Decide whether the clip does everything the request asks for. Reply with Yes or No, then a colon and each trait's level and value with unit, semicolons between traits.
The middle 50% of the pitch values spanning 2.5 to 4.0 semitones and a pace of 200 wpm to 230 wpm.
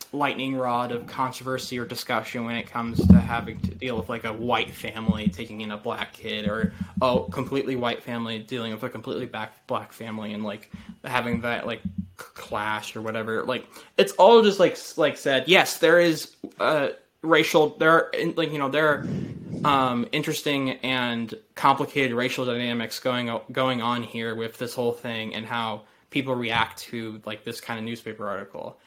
No: average, 2.9 semitones; average, 185 wpm